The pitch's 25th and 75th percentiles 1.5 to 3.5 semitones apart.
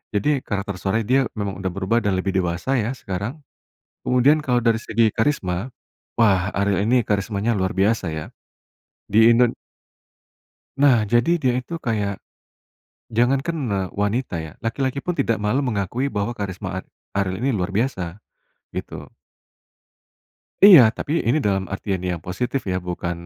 No: average, 4.2 semitones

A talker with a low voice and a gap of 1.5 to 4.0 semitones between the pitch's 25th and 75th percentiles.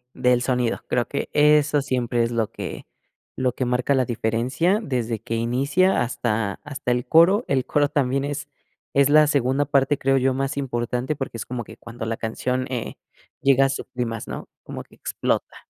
Yes: low, 130 Hz; average, 2.8 semitones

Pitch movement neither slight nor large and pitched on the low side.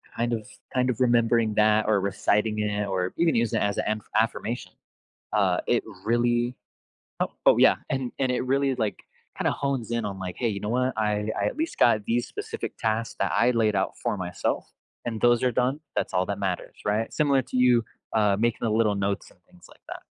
Yes: average, 3.0 semitones; low, 115 Hz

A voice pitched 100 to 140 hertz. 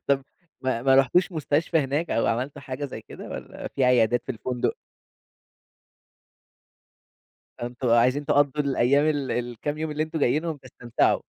Yes: low, 135 Hz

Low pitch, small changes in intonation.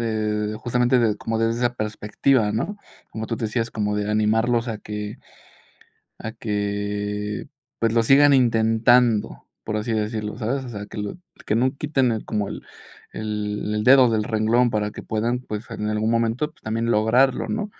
Yes: low, 110 Hz; narrow, 2.2 semitones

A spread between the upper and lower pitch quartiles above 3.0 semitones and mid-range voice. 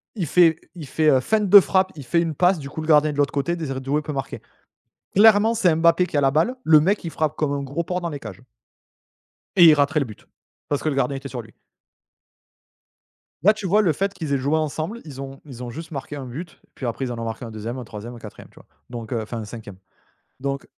Yes: average, 4.4 semitones; medium, 145 Hz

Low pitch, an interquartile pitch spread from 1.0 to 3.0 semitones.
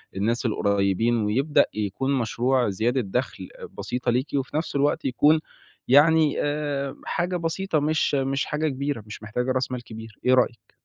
No: low, 130 Hz; average, 4.1 semitones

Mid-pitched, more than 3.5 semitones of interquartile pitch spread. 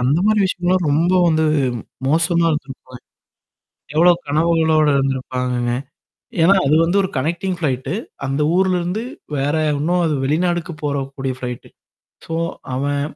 Yes: medium, 155 Hz; average, 4.1 semitones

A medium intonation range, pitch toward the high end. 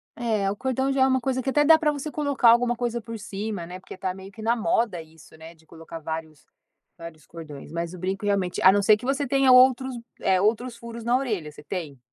No: wide, 6.7 semitones; high, 215 Hz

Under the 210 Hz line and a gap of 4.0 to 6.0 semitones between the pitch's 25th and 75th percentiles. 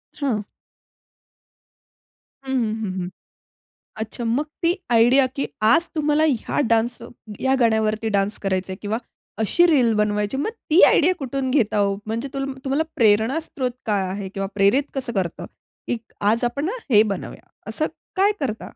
No: high, 235 Hz; average, 4.7 semitones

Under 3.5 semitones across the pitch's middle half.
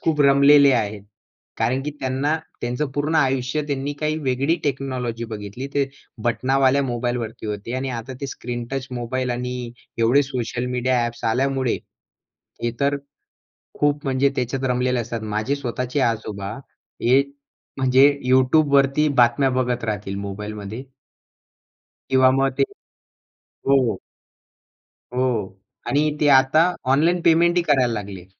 Yes: average, 2.8 semitones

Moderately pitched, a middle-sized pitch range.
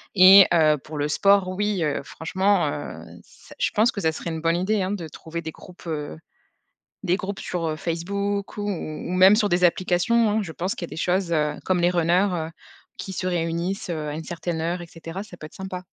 Yes: medium, 175 Hz; average, 3.0 semitones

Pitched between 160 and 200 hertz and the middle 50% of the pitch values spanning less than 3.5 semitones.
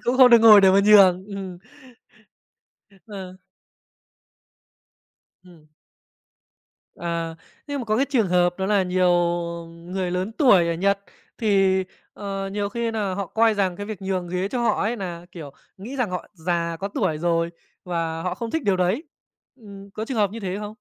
Yes: high, 195 Hz; average, 3.1 semitones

